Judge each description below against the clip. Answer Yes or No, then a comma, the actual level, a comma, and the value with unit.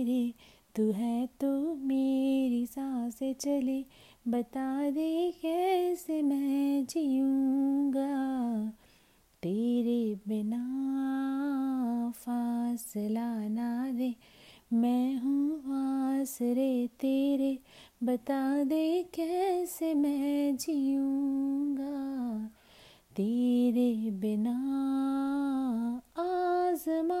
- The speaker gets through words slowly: Yes, slow, 65 wpm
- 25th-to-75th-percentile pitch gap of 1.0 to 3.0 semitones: Yes, average, 2.7 semitones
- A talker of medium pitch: No, very high, 270 Hz